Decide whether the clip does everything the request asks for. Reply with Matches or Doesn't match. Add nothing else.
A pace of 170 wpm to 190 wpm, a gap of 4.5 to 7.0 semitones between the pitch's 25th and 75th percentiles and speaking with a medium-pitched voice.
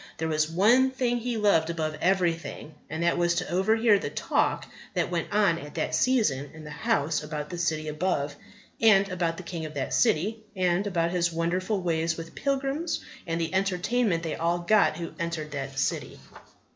Doesn't match